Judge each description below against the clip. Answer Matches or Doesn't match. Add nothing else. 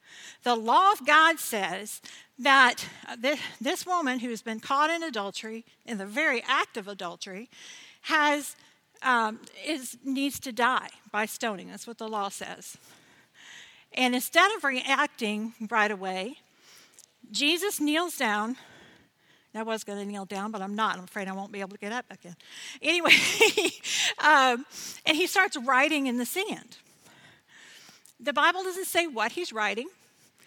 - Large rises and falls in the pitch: Matches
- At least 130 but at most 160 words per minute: Matches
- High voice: Matches